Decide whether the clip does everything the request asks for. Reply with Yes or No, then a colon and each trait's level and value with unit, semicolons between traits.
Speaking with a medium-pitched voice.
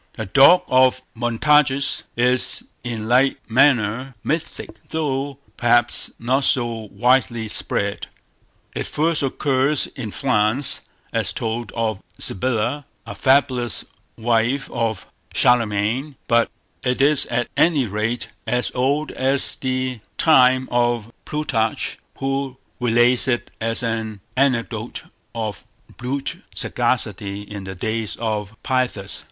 No: low, 120 Hz